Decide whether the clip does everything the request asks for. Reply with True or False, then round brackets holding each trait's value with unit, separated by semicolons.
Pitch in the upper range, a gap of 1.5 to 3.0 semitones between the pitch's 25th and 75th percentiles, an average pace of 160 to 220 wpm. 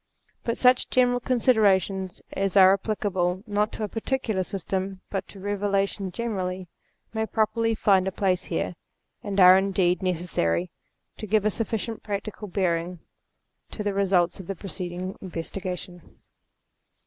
False (195 Hz; 2.6 semitones; 140 wpm)